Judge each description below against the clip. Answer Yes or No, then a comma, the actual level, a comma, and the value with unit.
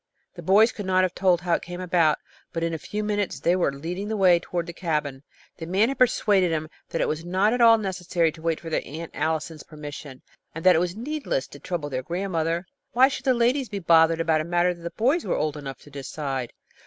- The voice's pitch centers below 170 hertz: No, medium, 175 Hz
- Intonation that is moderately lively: Yes, average, 3.6 semitones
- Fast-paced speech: Yes, fast, 240 wpm